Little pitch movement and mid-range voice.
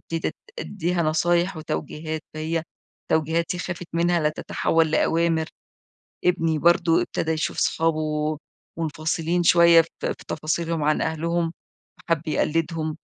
Yes: narrow, 1.4 semitones; medium, 165 Hz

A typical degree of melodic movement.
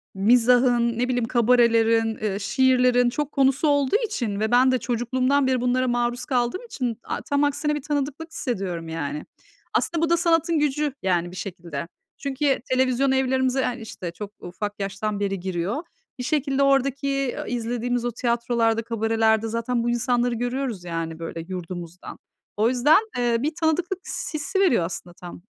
Yes: average, 3.9 semitones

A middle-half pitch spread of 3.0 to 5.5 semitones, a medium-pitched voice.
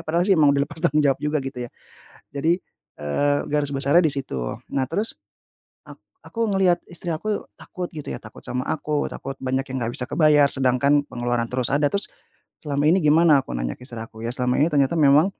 Yes: average, 3.6 semitones; medium, 145 Hz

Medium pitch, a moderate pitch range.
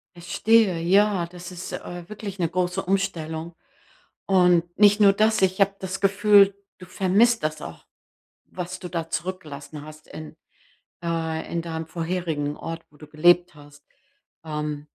Yes: medium, 175 Hz; average, 3.2 semitones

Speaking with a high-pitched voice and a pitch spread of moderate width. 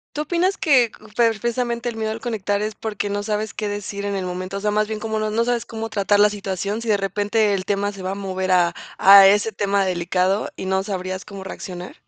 No: high, 205 Hz; narrow, 2.3 semitones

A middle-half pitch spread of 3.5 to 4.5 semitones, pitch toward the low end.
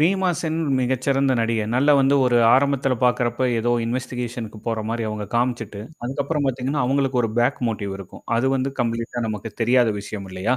No: average, 2.8 semitones; low, 125 Hz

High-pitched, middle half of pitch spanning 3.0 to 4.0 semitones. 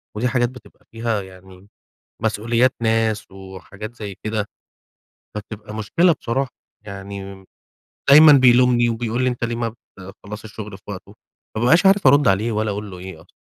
No: low, 110 Hz; average, 3.4 semitones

